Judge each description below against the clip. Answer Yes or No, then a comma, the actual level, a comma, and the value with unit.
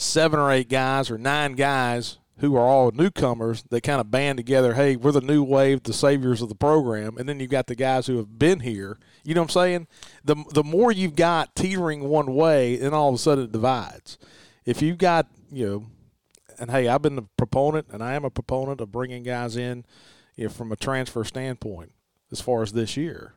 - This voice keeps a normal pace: No, fast, 225 wpm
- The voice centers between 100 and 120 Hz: No, low, 130 Hz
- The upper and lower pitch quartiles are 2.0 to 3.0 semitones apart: No, average, 3.6 semitones